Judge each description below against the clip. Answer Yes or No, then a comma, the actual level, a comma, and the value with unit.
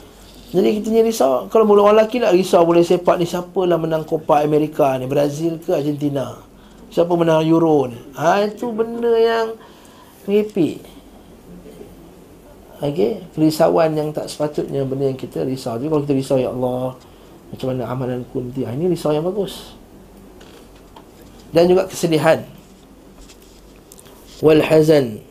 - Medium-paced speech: Yes, average, 140 wpm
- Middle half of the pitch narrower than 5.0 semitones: No, wide, 5.4 semitones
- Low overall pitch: No, medium, 160 Hz